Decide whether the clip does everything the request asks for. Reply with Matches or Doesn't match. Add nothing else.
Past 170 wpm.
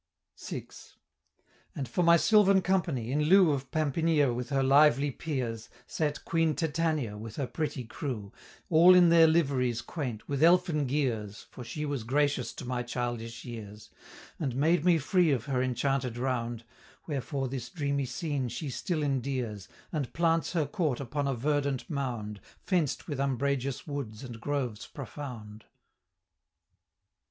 Doesn't match